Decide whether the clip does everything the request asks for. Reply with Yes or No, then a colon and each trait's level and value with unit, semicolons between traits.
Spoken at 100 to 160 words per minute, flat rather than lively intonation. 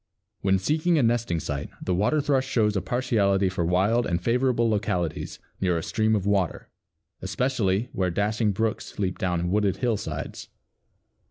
No: average, 155 wpm; average, 4.3 semitones